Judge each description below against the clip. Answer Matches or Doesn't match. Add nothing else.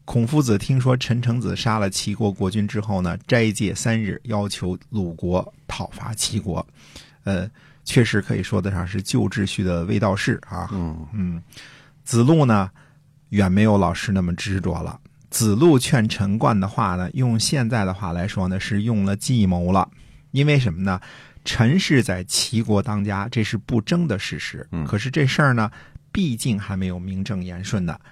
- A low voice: Matches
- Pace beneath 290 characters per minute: Matches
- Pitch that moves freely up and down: Doesn't match